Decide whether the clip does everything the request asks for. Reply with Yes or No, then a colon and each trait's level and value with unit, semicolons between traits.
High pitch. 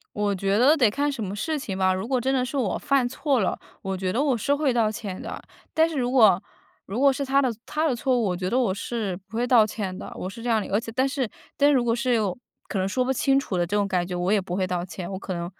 Yes: high, 230 Hz